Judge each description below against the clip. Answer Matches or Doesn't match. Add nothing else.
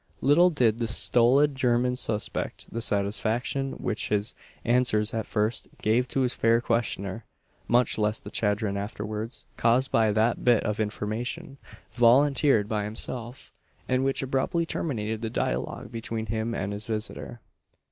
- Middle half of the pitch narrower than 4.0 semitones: Matches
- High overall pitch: Doesn't match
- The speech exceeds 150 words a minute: Doesn't match